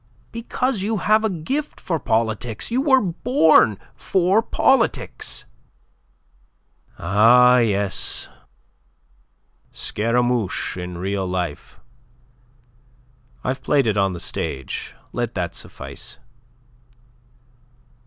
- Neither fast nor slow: No, slow, 90 wpm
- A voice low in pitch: Yes, low, 125 Hz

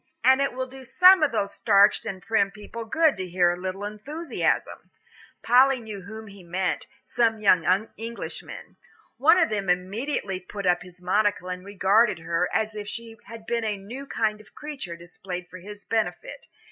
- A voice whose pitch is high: Yes, high, 210 Hz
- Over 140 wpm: Yes, average, 180 wpm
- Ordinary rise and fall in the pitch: Yes, average, 4.0 semitones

